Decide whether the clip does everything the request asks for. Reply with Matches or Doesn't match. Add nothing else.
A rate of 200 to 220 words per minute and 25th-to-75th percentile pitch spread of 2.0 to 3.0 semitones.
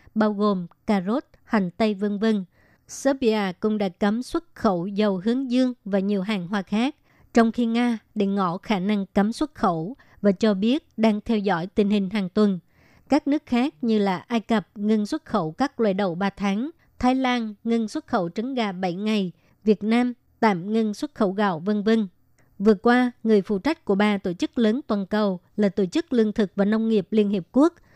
Matches